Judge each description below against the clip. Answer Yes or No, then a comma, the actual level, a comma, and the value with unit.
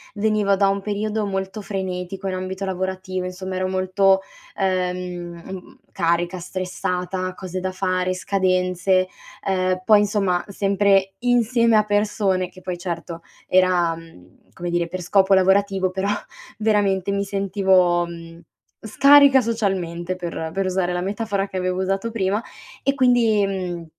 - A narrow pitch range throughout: Yes, narrow, 1.7 semitones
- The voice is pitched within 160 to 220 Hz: Yes, high, 190 Hz